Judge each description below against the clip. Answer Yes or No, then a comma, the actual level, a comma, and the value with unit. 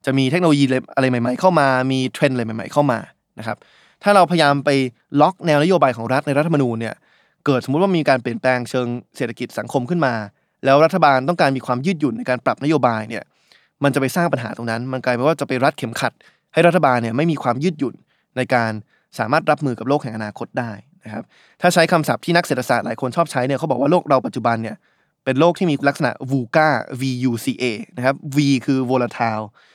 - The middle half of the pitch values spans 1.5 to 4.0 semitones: Yes, average, 3.6 semitones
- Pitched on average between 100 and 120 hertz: No, low, 135 Hz